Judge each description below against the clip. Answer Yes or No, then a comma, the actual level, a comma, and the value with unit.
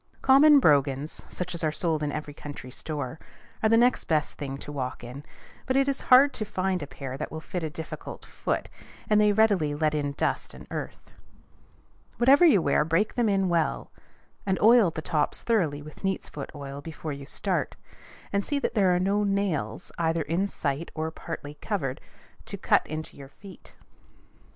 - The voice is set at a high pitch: No, medium, 165 Hz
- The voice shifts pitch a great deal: Yes, wide, 5.8 semitones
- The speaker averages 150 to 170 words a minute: No, average, 185 wpm